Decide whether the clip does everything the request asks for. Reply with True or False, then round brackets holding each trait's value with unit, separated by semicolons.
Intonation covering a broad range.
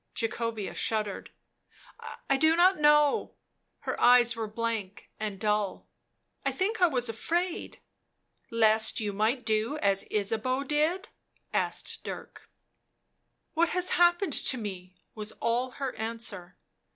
True (5.8 semitones)